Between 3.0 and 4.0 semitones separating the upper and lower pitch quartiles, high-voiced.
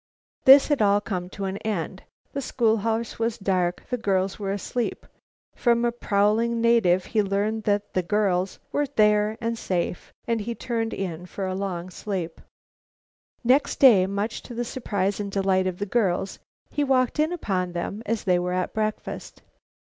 Yes: average, 3.6 semitones; high, 205 Hz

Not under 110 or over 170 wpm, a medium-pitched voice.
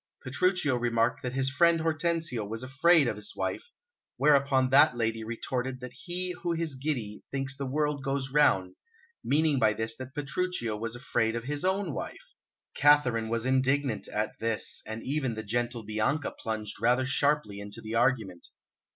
No: average, 165 wpm; low, 130 Hz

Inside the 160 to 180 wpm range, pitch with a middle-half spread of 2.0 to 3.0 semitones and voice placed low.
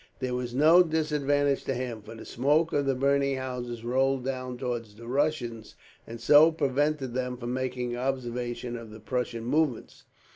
Yes: average, 170 wpm; average, 2.7 semitones; low, 130 Hz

